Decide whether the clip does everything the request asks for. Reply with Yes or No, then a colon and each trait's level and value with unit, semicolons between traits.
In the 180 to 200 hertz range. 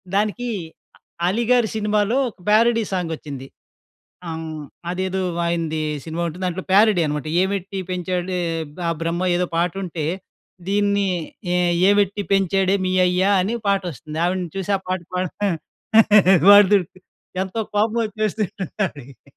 Yes: high, 190 Hz